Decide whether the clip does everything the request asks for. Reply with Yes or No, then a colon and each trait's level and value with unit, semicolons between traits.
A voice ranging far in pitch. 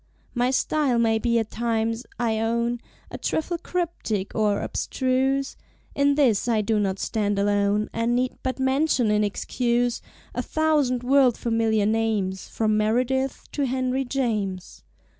No: average, 3.5 semitones